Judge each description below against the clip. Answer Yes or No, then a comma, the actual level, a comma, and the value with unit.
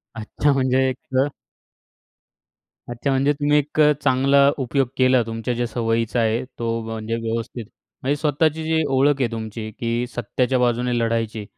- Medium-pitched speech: No, low, 125 Hz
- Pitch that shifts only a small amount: No, average, 3.1 semitones